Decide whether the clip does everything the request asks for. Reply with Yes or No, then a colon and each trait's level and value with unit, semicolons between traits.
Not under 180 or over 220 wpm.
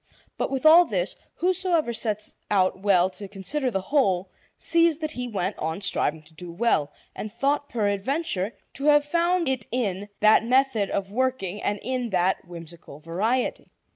No: average, 165 wpm